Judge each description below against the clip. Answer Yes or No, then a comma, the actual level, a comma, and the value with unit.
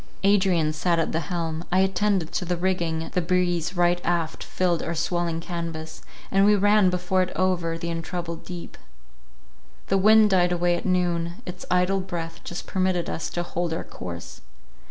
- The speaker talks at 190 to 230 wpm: No, average, 175 wpm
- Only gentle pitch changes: Yes, narrow, 1.8 semitones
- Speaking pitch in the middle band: Yes, medium, 175 Hz